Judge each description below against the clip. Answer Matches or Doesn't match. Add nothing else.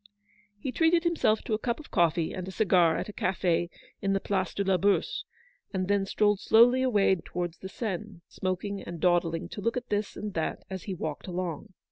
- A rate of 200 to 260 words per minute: Matches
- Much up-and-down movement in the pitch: Doesn't match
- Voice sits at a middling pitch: Doesn't match